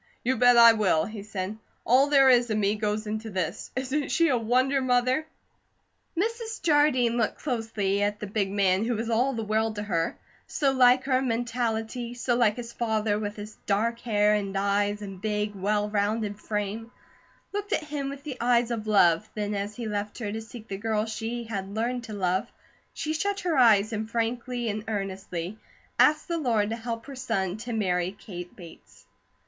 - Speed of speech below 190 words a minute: No, average, 195 wpm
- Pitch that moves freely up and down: No, average, 3.2 semitones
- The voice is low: No, high, 220 Hz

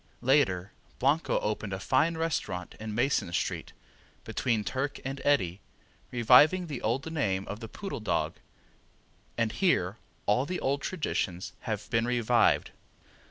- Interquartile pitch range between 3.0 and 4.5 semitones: No, wide, 5.4 semitones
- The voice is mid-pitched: No, low, 120 Hz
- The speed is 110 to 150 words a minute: Yes, slow, 135 wpm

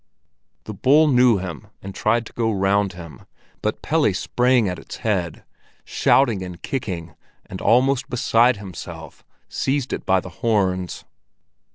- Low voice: Yes, low, 105 Hz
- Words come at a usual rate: Yes, average, 145 wpm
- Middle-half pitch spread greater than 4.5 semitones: Yes, average, 5.0 semitones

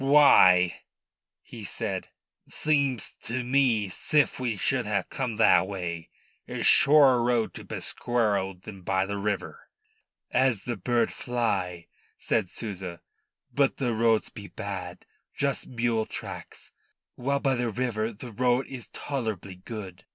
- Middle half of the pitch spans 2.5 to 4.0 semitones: No, average, 4.6 semitones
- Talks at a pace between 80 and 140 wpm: Yes, slow, 135 wpm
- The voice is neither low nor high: No, low, 115 Hz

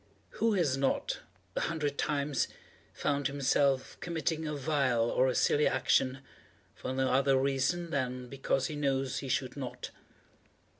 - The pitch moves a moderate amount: No, narrow, 2.0 semitones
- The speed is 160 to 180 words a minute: No, average, 145 wpm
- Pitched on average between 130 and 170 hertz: Yes, low, 135 Hz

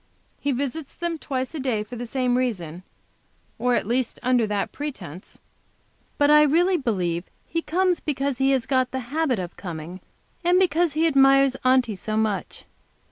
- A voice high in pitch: Yes, very high, 260 Hz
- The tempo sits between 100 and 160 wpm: No, average, 170 wpm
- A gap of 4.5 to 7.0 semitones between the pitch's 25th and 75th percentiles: Yes, average, 5.2 semitones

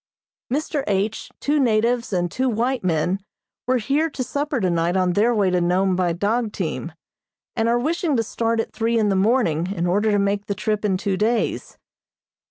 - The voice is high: Yes, high, 210 Hz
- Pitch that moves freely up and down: No, average, 4.5 semitones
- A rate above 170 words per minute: Yes, average, 190 wpm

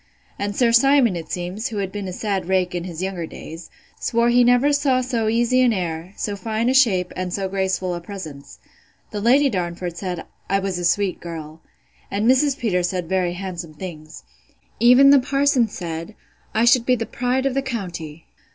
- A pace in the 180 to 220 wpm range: Yes, average, 190 wpm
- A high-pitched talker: Yes, high, 195 Hz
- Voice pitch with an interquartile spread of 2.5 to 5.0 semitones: No, wide, 5.4 semitones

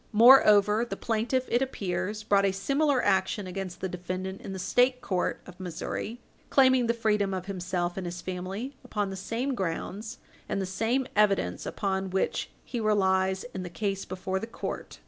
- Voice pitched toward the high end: Yes, high, 195 Hz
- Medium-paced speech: Yes, average, 175 wpm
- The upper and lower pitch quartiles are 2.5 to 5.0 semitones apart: Yes, average, 3.5 semitones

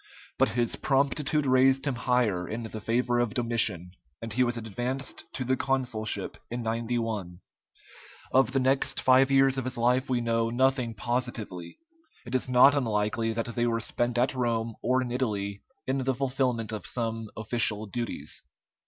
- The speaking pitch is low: Yes, low, 120 Hz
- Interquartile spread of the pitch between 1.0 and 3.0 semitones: Yes, narrow, 2.4 semitones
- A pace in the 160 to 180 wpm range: Yes, average, 165 wpm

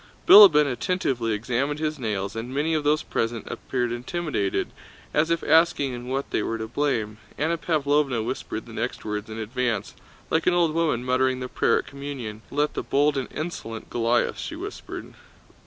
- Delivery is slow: No, average, 175 wpm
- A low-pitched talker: Yes, low, 130 Hz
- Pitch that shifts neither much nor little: Yes, average, 4.8 semitones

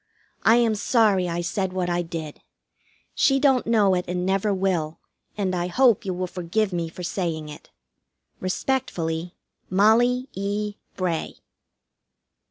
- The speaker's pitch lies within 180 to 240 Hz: Yes, medium, 185 Hz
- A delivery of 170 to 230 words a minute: No, average, 140 wpm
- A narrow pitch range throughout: No, average, 3.6 semitones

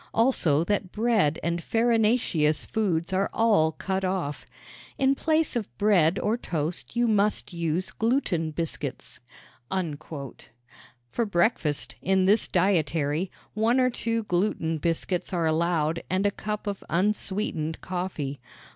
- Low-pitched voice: No, medium, 185 Hz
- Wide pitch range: No, average, 4.9 semitones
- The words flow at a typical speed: No, slow, 125 wpm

